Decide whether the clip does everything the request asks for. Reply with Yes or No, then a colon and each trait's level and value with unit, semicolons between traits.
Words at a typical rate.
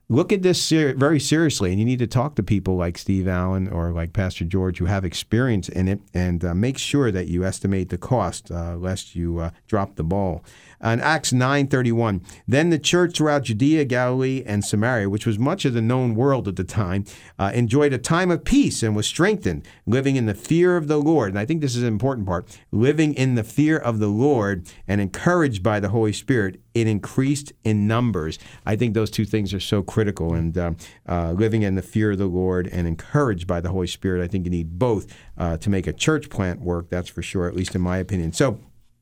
No: fast, 225 wpm